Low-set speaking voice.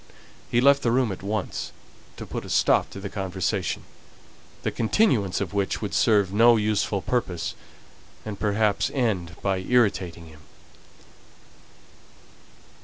Yes: low, 100 Hz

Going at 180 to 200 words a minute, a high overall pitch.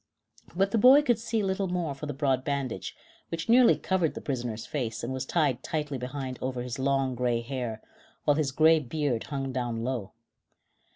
No: average, 185 wpm; low, 135 Hz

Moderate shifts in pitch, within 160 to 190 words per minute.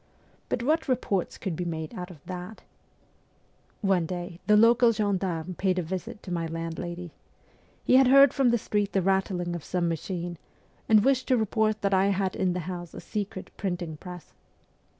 Yes: average, 3.3 semitones; average, 180 wpm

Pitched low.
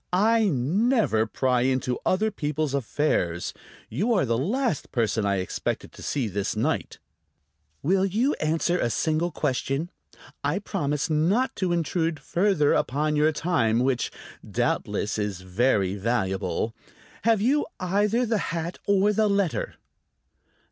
No: medium, 155 Hz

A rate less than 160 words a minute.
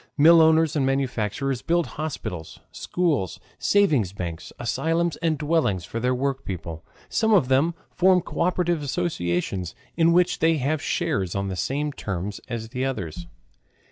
Yes: average, 140 wpm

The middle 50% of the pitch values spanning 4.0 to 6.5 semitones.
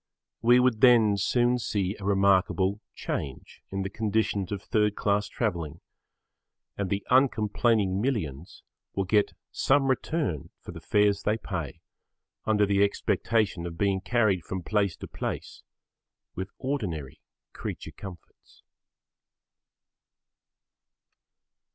No: average, 2.9 semitones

